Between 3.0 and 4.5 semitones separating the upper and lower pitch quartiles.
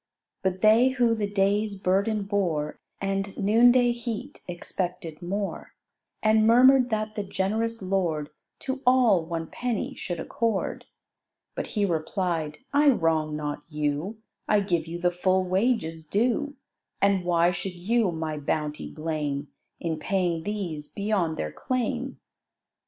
No: average, 5.0 semitones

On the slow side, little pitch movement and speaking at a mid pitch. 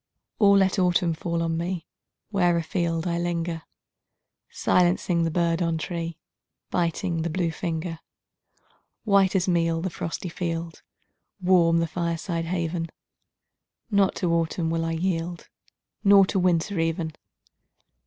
Yes: slow, 130 wpm; narrow, 1.6 semitones; medium, 170 Hz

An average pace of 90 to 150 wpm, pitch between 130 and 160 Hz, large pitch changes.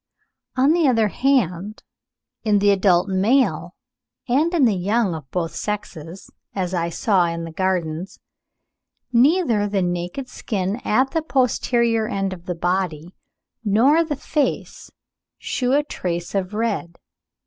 No: slow, 135 wpm; high, 205 Hz; wide, 5.9 semitones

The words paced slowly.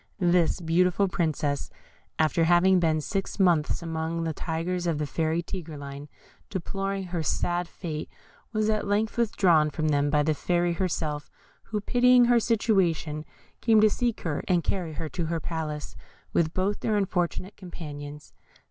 No: average, 155 wpm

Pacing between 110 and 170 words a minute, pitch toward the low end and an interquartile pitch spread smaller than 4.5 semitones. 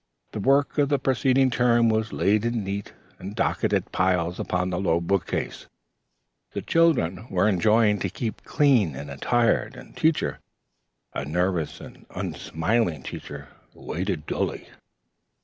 No: average, 140 wpm; low, 100 Hz; wide, 5.5 semitones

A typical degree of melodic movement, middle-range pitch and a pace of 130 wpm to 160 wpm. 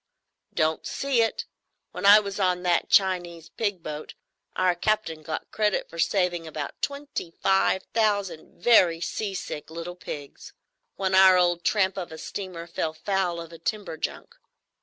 Yes: average, 3.2 semitones; medium, 180 Hz; average, 155 wpm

